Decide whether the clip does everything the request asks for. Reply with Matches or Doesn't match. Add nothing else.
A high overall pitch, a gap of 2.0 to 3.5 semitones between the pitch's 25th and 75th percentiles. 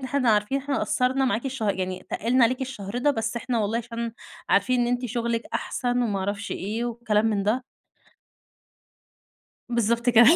Matches